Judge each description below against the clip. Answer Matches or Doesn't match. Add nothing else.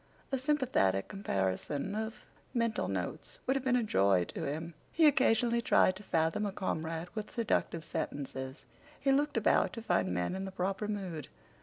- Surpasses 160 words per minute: Matches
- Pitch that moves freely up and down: Matches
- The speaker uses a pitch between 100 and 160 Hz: Doesn't match